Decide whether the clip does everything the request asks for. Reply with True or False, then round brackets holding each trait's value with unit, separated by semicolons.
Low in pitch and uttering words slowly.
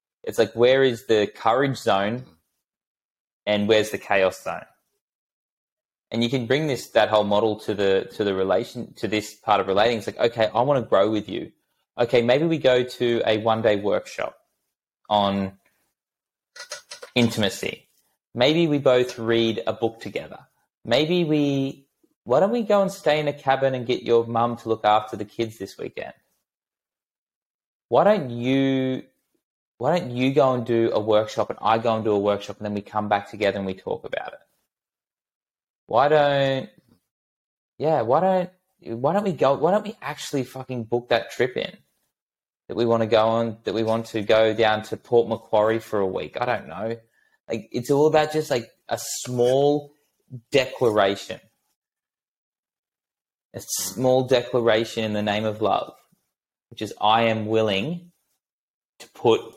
False (115 Hz; 170 wpm)